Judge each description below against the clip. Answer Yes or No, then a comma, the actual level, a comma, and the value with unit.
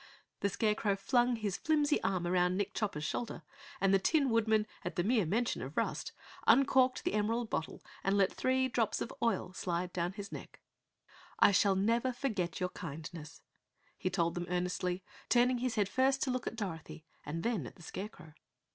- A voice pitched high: Yes, high, 200 Hz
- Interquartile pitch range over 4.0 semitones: Yes, average, 5.0 semitones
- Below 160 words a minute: No, average, 180 wpm